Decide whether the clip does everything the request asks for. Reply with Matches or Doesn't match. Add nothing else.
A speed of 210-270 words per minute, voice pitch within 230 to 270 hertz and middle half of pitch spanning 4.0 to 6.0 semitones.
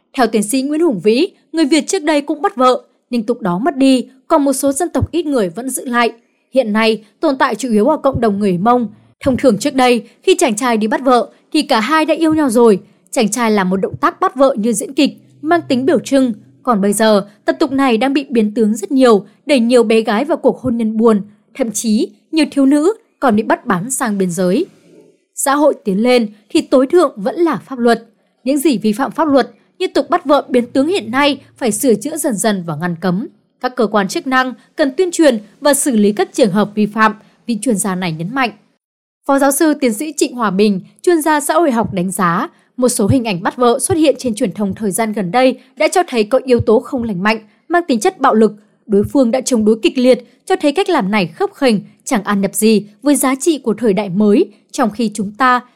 Matches